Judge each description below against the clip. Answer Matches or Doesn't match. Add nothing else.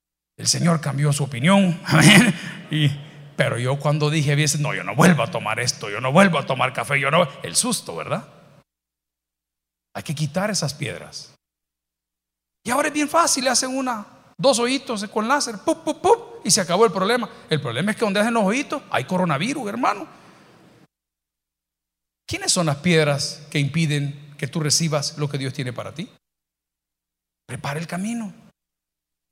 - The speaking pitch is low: Doesn't match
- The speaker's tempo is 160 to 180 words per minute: Matches